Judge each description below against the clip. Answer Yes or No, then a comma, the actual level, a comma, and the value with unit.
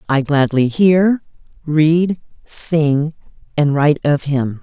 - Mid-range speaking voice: Yes, medium, 150 Hz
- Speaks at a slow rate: Yes, slow, 115 wpm